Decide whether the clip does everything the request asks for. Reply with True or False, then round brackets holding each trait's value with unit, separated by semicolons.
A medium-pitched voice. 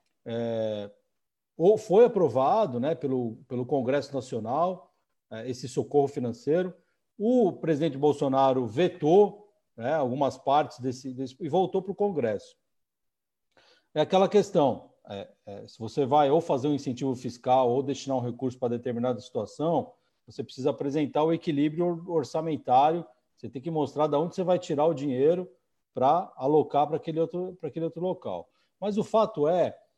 True (150 Hz)